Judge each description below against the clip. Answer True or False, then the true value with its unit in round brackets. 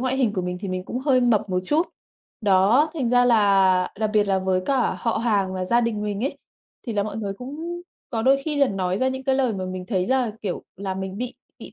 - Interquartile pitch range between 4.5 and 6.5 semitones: True (5.2 semitones)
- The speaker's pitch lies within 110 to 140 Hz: False (215 Hz)